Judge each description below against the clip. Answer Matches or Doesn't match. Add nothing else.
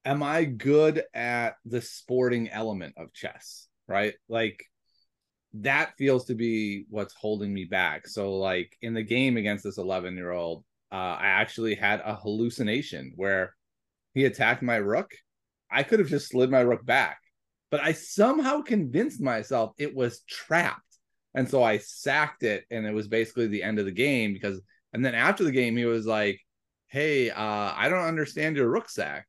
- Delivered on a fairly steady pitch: Doesn't match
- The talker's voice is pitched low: Matches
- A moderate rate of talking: Matches